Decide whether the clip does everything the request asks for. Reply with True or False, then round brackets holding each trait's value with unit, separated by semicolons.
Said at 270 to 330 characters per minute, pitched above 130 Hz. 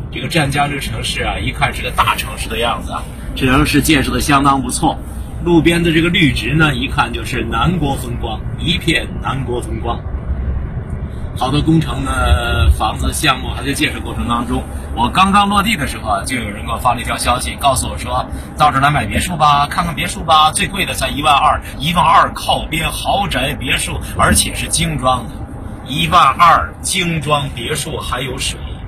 True (285 characters per minute; 140 Hz)